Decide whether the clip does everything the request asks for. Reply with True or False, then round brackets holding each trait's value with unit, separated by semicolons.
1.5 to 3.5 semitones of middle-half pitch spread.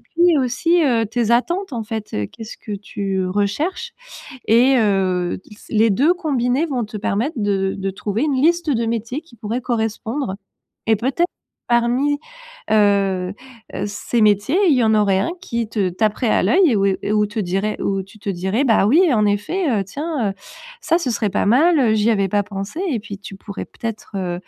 False (4.6 semitones)